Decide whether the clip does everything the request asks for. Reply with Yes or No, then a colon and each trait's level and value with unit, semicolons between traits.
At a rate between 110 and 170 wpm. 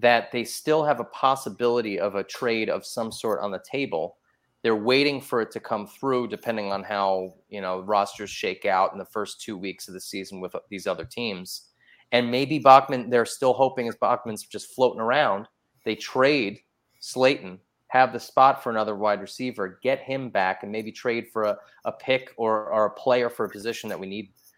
No: fast, 205 wpm